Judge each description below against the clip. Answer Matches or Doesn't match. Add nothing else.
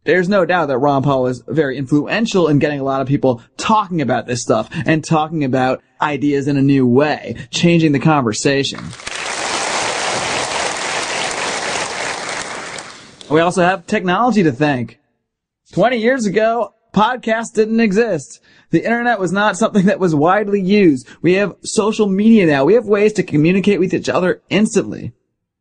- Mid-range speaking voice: Matches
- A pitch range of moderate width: Doesn't match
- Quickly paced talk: Doesn't match